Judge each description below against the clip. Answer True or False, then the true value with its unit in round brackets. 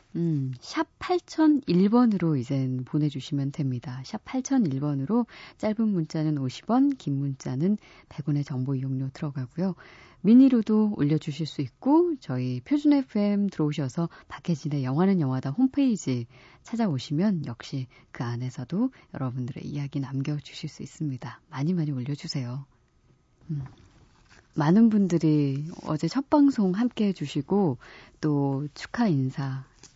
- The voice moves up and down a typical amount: False (7.3 semitones)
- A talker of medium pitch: True (150 Hz)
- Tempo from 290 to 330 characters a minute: False (275 characters per minute)